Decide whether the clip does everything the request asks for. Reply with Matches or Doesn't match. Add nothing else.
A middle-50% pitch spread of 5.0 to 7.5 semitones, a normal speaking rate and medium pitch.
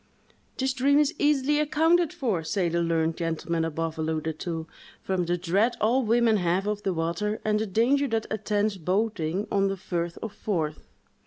Doesn't match